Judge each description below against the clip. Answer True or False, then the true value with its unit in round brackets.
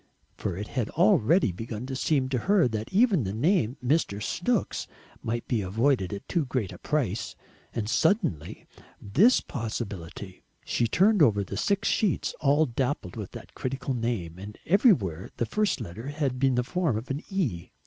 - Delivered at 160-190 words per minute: True (170 wpm)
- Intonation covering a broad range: True (6.7 semitones)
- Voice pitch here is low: True (125 Hz)